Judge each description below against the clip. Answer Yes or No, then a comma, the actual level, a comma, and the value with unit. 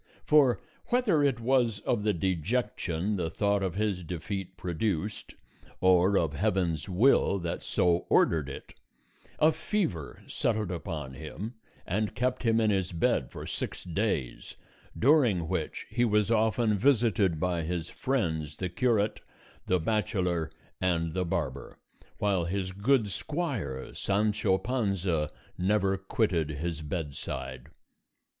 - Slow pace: Yes, slow, 130 wpm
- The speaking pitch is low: Yes, very low, 95 Hz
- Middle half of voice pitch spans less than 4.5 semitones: No, average, 4.8 semitones